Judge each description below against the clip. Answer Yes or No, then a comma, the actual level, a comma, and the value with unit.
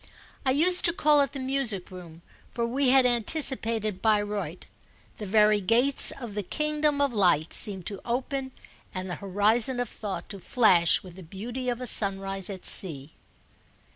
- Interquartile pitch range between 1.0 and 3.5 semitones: No, average, 5.3 semitones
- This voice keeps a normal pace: Yes, average, 170 wpm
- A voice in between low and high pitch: No, high, 215 Hz